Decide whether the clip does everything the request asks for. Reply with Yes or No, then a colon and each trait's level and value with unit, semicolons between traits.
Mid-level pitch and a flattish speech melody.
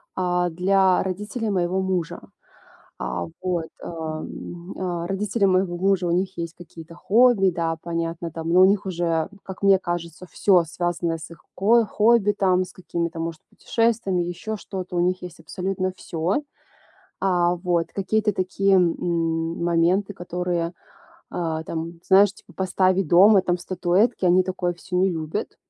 Yes: medium, 180 Hz; narrow, 2.2 semitones